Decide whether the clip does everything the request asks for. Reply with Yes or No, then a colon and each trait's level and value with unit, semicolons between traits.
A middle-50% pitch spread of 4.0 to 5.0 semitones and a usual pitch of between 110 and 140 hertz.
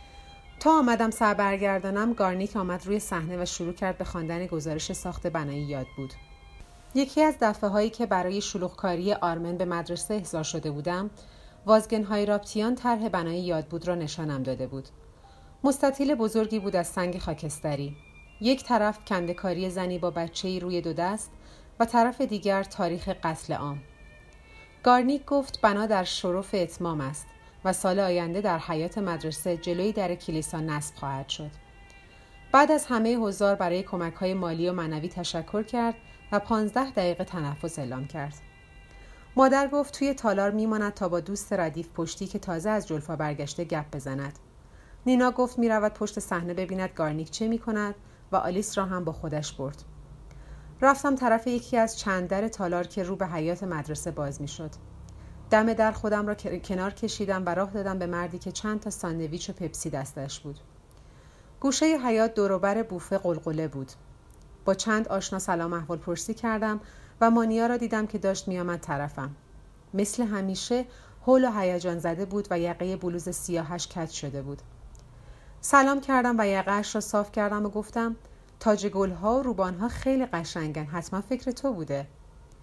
No: average, 4.4 semitones; medium, 185 Hz